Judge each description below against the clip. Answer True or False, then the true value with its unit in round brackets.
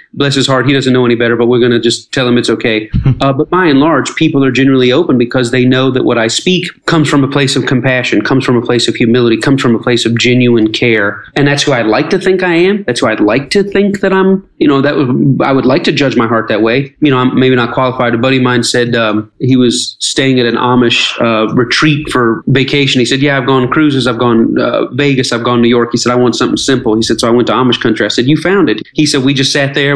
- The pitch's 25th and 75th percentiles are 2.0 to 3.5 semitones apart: True (3.0 semitones)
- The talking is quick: True (290 wpm)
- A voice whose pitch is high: False (130 Hz)